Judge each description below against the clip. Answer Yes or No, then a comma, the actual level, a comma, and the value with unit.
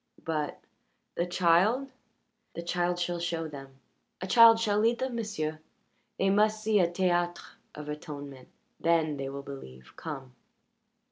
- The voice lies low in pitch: No, medium, 170 Hz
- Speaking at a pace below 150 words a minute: Yes, average, 140 wpm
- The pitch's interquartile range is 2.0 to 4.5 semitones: No, wide, 5.4 semitones